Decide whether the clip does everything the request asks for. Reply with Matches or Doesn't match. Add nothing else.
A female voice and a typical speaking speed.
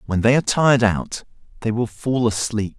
Doesn't match